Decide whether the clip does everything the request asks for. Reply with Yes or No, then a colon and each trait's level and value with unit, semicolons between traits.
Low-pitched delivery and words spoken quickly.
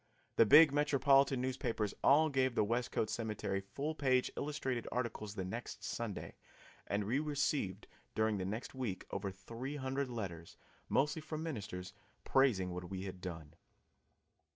No: low, 120 Hz; average, 145 wpm